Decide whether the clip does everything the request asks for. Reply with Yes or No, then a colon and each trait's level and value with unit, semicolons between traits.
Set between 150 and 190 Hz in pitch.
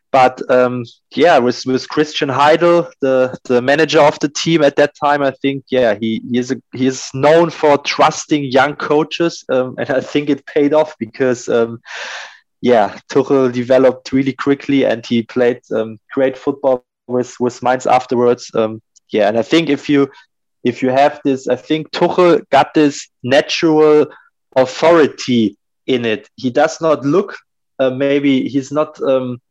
No: low, 135 Hz